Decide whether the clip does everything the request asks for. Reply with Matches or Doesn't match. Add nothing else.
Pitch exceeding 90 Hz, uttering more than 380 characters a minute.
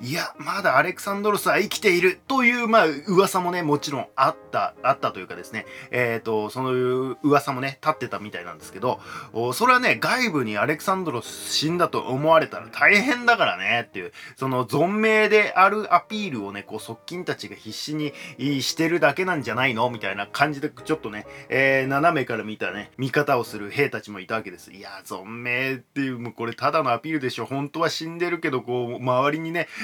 Matches